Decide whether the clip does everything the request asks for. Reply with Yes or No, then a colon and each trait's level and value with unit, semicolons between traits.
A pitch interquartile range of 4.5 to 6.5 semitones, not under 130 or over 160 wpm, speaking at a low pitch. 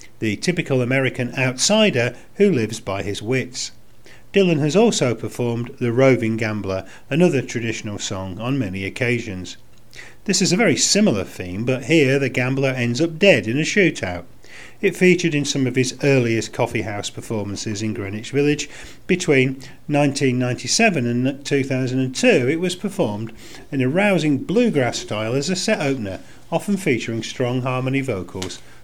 Yes: average, 5.0 semitones; average, 150 wpm; low, 130 Hz